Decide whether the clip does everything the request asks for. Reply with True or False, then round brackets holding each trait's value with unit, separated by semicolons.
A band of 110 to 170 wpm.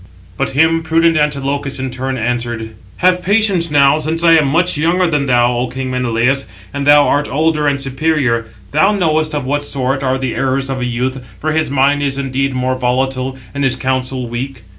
False (195 wpm)